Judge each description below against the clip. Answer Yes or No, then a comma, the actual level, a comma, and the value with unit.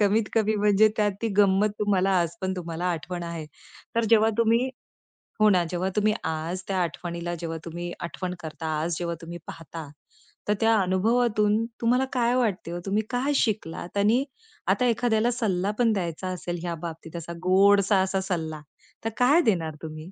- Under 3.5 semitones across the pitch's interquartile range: No, average, 4.2 semitones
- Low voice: No, high, 190 Hz